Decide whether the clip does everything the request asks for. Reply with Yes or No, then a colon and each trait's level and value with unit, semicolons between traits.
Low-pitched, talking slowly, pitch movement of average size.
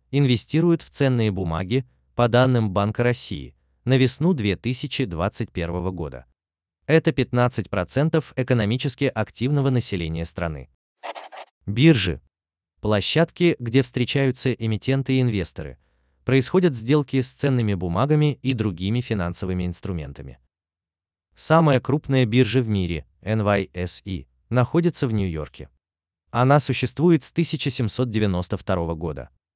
No: low, 110 Hz; slow, 95 wpm; wide, 7.4 semitones